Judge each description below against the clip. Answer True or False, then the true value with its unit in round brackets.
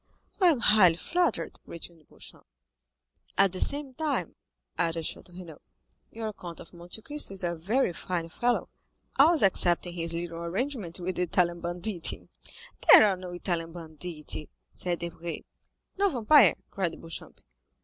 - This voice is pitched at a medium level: True (180 Hz)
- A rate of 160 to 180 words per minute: False (145 wpm)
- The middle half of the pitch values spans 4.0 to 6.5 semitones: True (4.5 semitones)